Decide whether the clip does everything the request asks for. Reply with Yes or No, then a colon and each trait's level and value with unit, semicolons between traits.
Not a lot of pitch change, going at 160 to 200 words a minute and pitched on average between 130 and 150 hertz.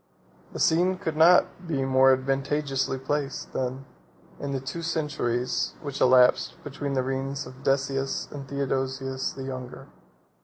No: narrow, 1.7 semitones; average, 145 wpm; low, 135 Hz